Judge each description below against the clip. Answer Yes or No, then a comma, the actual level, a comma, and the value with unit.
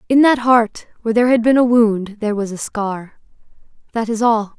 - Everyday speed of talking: No, fast, 210 wpm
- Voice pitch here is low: No, high, 225 Hz